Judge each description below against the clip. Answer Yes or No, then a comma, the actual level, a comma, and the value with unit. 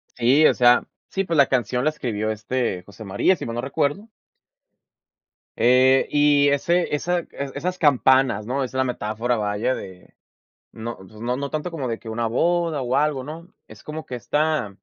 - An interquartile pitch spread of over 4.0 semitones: Yes, average, 4.7 semitones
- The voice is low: Yes, low, 130 Hz